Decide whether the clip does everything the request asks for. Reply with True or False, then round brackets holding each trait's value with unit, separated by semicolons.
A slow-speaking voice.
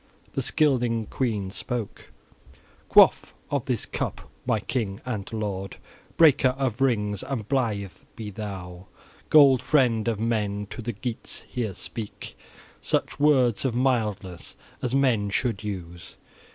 True (130 wpm)